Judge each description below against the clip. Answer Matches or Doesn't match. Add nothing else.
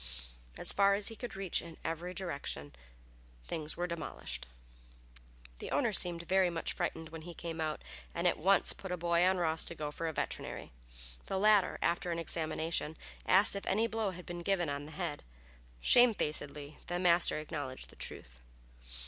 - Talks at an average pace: Matches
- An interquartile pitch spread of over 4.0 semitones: Doesn't match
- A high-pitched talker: Doesn't match